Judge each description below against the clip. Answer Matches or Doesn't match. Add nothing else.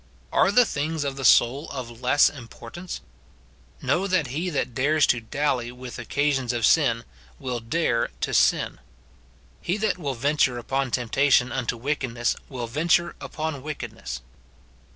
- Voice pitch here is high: Doesn't match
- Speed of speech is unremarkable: Matches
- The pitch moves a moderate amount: Matches